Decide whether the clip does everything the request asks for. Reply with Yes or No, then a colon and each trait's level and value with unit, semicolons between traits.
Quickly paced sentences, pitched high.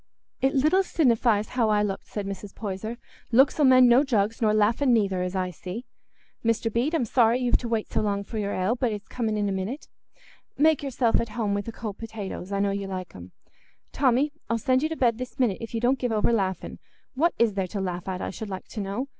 Yes: fast, 240 wpm; high, 225 Hz